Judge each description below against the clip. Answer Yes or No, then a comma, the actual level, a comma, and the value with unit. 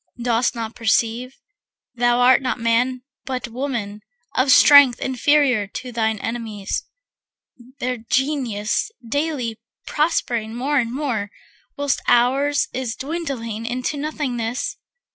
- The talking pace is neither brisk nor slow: No, slow, 110 wpm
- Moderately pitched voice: No, high, 245 Hz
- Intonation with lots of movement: No, average, 3.2 semitones